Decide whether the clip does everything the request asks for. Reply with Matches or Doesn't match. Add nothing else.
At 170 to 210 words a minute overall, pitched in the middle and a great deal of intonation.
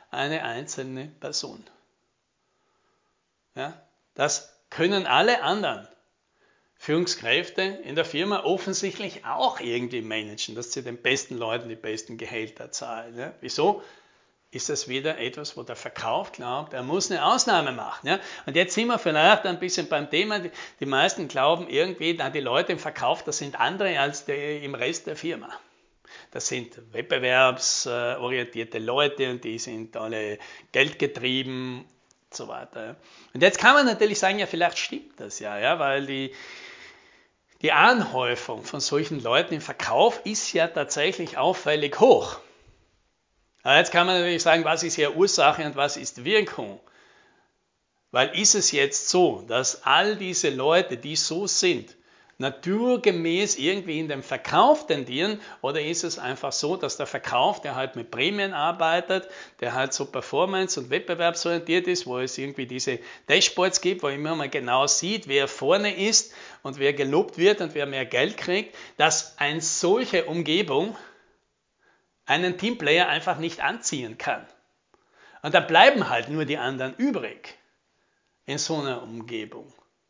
Doesn't match